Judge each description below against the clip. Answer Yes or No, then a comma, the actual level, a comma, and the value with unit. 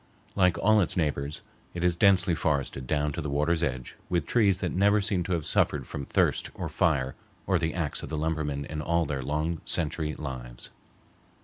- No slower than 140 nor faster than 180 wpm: No, average, 195 wpm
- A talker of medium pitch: No, very low, 80 Hz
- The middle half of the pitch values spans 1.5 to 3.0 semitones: No, average, 3.7 semitones